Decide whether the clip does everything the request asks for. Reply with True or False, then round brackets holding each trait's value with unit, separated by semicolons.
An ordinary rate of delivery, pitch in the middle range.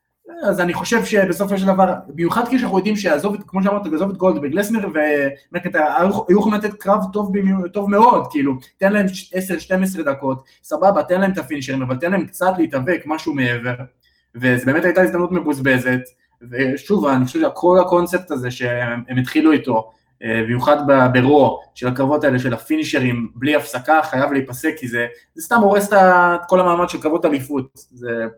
False (165 wpm; 155 Hz)